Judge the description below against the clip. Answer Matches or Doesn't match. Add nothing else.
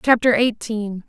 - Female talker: Matches